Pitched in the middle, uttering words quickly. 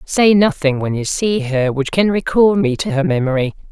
Yes: medium, 160 Hz; fast, 210 wpm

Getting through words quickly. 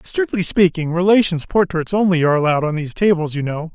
No: average, 190 wpm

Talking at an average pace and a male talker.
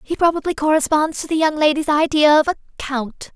No: average, 195 wpm; female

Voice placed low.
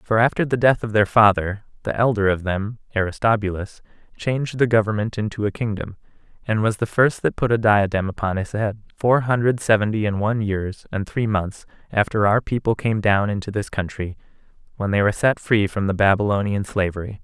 Yes: low, 105 Hz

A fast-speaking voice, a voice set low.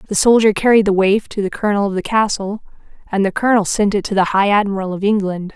No: fast, 240 wpm; high, 205 Hz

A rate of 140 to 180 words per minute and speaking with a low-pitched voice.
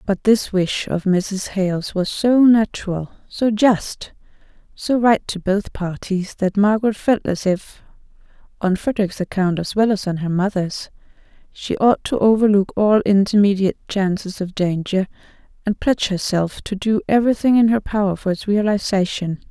No: average, 155 wpm; high, 200 Hz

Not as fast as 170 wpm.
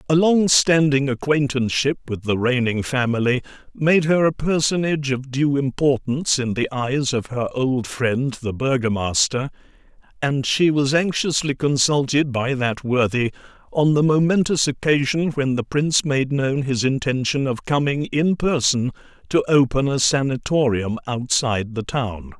Yes: average, 140 wpm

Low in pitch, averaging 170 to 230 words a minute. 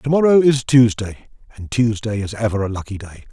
Yes: low, 115 Hz; average, 200 wpm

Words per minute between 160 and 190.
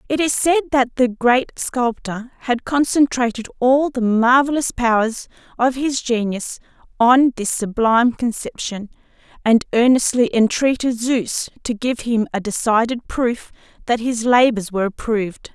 No: slow, 135 wpm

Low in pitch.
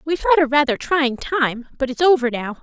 No: very high, 280 Hz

